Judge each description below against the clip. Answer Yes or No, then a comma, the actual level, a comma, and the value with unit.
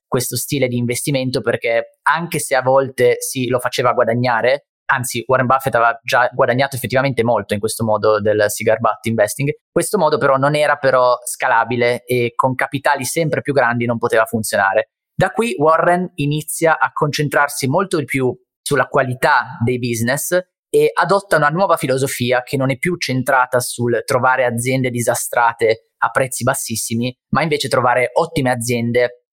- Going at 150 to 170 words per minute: Yes, average, 160 wpm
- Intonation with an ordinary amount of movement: Yes, average, 3.6 semitones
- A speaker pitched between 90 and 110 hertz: No, low, 130 Hz